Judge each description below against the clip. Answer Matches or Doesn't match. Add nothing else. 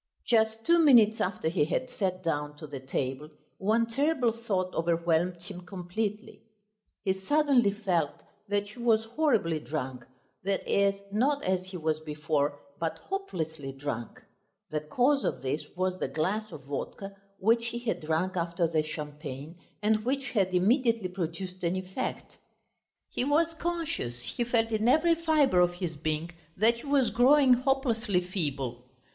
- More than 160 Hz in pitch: Matches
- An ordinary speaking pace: Matches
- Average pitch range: Doesn't match